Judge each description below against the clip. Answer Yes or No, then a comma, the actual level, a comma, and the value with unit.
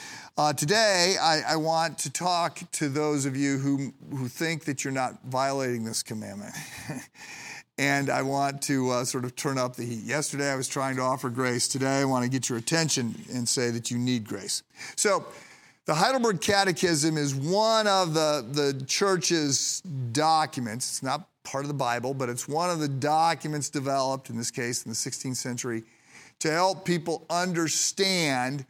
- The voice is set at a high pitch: No, medium, 140 Hz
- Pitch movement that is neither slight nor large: Yes, average, 3.9 semitones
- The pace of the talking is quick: No, average, 180 wpm